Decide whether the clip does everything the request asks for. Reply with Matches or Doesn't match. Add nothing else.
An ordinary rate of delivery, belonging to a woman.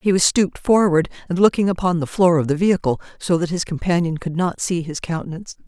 Doesn't match